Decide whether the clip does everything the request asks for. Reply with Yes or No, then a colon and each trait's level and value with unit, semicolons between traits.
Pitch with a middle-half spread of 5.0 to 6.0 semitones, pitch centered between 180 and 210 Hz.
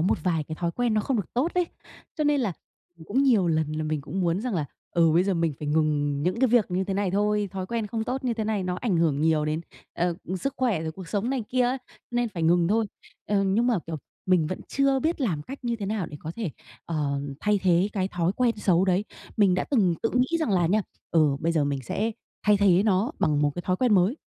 Yes: wide, 5.5 semitones; high, 190 Hz